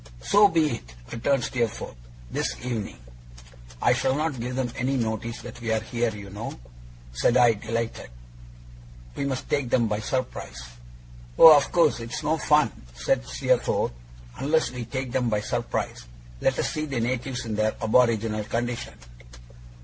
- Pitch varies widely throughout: No, average, 3.1 semitones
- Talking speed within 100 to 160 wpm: Yes, average, 155 wpm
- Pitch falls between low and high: No, low, 120 Hz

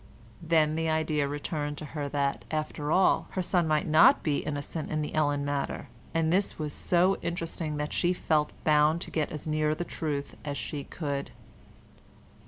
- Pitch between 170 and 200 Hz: No, medium, 155 Hz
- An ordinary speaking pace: Yes, average, 175 wpm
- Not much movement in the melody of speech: Yes, narrow, 1.8 semitones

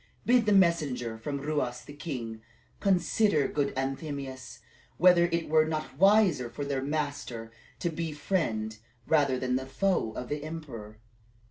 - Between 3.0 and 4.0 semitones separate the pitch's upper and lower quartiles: No, average, 4.8 semitones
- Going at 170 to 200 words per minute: No, average, 150 wpm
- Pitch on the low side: No, medium, 145 Hz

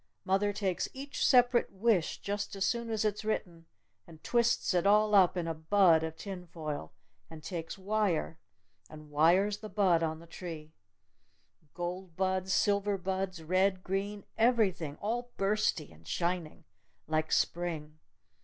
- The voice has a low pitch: No, medium, 185 Hz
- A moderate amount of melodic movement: Yes, average, 3.9 semitones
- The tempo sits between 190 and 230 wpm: No, average, 145 wpm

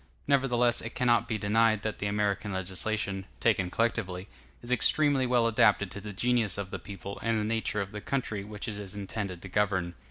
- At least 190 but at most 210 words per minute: Yes, average, 195 wpm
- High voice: No, low, 105 Hz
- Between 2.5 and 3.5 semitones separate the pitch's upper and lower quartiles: Yes, average, 2.8 semitones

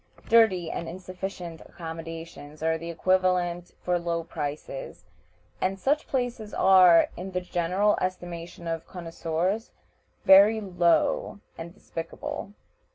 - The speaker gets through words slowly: Yes, slow, 110 wpm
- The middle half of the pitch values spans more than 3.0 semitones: No, narrow, 2.4 semitones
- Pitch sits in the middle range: Yes, medium, 180 Hz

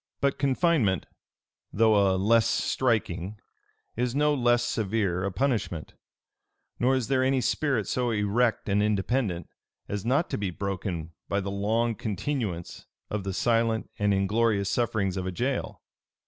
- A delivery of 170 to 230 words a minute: No, average, 145 wpm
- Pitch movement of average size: Yes, average, 3.9 semitones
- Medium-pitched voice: No, low, 110 Hz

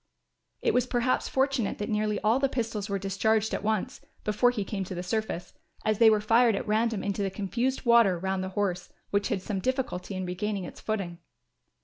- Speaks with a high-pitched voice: Yes, high, 210 Hz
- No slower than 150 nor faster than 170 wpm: No, fast, 205 wpm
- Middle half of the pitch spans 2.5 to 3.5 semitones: Yes, average, 3.0 semitones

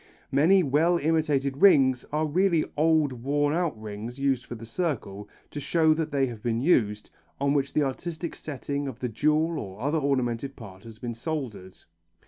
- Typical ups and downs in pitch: Yes, average, 4.8 semitones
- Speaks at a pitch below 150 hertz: Yes, medium, 140 Hz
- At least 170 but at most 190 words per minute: Yes, average, 175 wpm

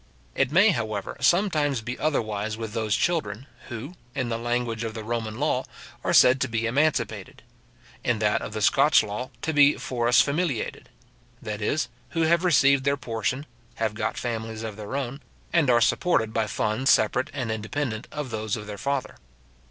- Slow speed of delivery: No, average, 175 wpm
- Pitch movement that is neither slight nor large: Yes, average, 4.4 semitones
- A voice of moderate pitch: No, low, 120 Hz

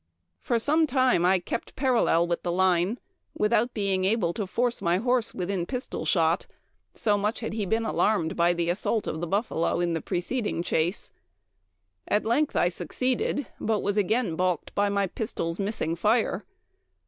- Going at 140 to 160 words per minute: No, average, 170 wpm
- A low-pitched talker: No, high, 200 Hz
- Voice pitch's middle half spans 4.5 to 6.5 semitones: Yes, average, 4.8 semitones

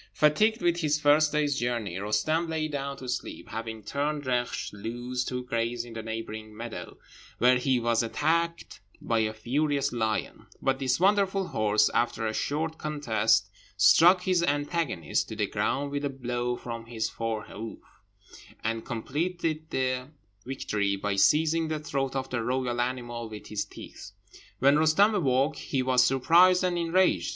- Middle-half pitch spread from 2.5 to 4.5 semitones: No, average, 5.1 semitones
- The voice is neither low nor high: No, low, 130 Hz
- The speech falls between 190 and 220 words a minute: No, average, 160 wpm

